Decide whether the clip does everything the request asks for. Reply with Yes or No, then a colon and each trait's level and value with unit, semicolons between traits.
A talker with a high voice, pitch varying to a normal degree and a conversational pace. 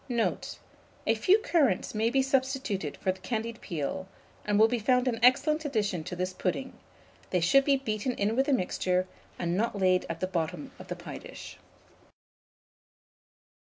No: high, 220 Hz; wide, 6.1 semitones; average, 170 wpm